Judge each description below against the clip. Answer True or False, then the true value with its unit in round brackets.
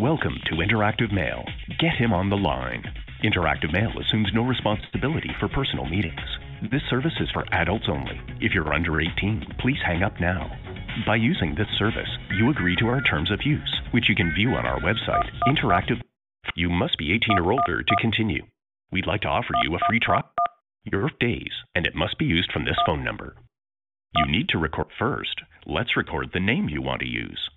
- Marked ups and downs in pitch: True (6.0 semitones)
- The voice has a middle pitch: False (105 Hz)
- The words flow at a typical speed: True (195 wpm)